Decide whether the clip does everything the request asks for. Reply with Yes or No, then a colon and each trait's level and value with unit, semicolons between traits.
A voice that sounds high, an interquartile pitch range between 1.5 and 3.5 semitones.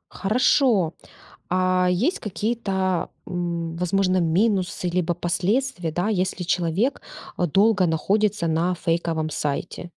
No: medium, 180 Hz; average, 3.1 semitones